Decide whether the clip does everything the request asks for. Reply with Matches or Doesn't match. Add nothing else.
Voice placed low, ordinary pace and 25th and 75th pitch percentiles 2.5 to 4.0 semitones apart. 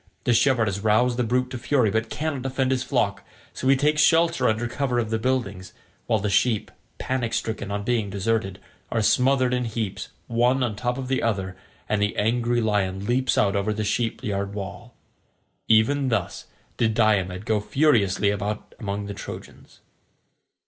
Matches